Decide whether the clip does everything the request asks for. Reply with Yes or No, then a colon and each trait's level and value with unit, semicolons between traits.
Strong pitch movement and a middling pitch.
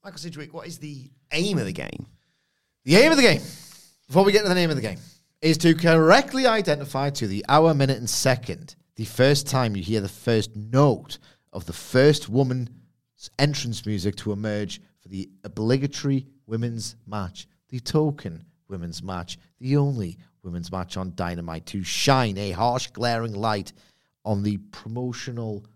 No: wide, 5.8 semitones; low, 120 Hz